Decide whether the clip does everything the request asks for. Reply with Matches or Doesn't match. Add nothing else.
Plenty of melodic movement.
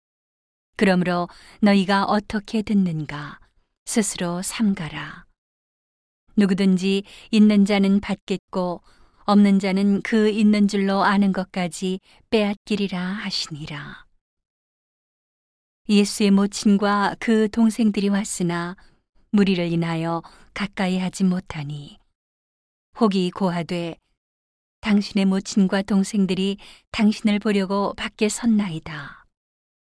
Doesn't match